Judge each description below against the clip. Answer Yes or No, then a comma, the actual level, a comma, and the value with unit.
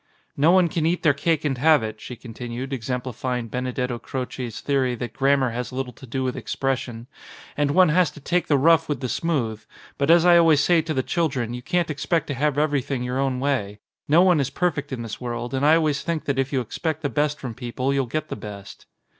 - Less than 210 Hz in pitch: Yes, low, 135 Hz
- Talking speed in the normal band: No, fast, 235 wpm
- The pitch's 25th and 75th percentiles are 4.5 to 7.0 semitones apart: No, average, 3.8 semitones